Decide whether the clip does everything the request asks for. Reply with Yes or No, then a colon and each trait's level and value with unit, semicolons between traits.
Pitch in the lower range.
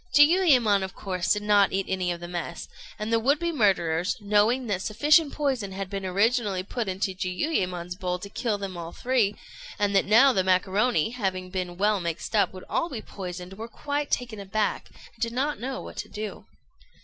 No: high, 205 Hz